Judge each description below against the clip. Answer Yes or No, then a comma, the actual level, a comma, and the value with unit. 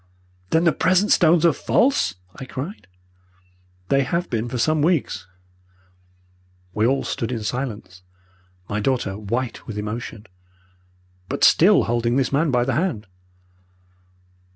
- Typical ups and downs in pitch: No, wide, 5.9 semitones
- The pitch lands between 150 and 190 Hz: No, low, 125 Hz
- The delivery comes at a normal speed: No, slow, 130 wpm